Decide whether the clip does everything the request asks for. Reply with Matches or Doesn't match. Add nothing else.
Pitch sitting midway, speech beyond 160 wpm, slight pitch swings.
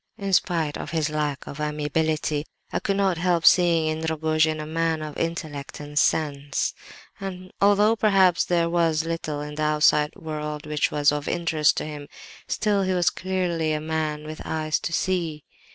Matches